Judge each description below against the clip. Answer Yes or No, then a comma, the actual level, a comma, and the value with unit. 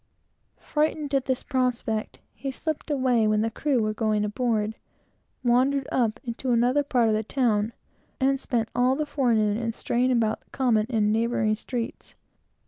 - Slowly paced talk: No, average, 165 wpm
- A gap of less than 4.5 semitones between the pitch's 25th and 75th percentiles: Yes, average, 3.2 semitones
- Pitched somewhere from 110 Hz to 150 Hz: No, high, 240 Hz